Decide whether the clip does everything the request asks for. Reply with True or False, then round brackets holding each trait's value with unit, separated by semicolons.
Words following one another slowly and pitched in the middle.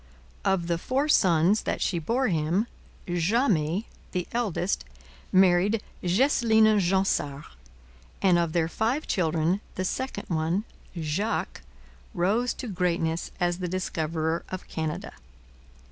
True (115 wpm; 180 Hz)